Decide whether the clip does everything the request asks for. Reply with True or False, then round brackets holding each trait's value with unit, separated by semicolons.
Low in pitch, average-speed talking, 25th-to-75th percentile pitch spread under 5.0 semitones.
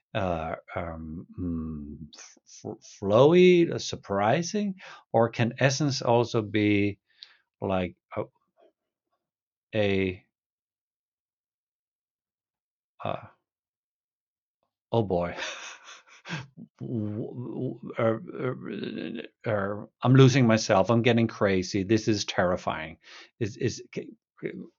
False (110 Hz; 70 wpm; 3.7 semitones)